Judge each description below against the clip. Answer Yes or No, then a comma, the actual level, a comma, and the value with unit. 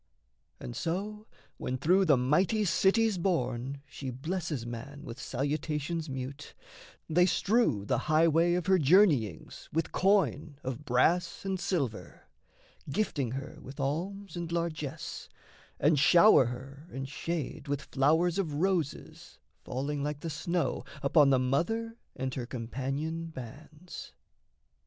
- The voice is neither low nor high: Yes, medium, 150 Hz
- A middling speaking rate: No, slow, 130 wpm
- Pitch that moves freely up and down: No, average, 4.6 semitones